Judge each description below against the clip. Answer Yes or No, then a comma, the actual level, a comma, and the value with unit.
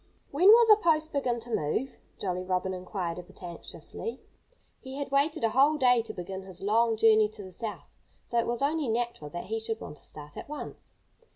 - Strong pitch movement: Yes, wide, 6.8 semitones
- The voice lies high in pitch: Yes, high, 225 Hz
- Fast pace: Yes, fast, 210 wpm